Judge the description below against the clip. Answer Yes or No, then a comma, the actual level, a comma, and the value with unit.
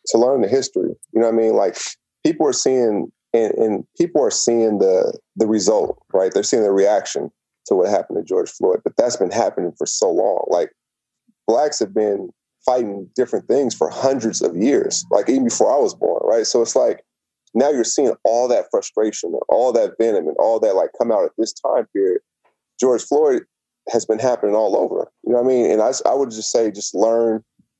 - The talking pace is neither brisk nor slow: No, fast, 215 wpm